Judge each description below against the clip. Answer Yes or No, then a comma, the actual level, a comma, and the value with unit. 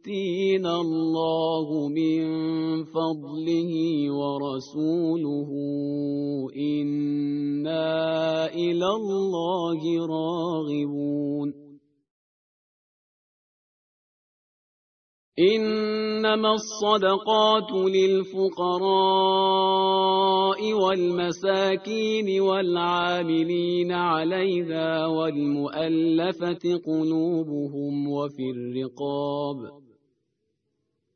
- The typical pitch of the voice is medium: Yes, medium, 165 Hz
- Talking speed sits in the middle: No, slow, 35 wpm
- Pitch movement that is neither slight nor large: Yes, average, 4.7 semitones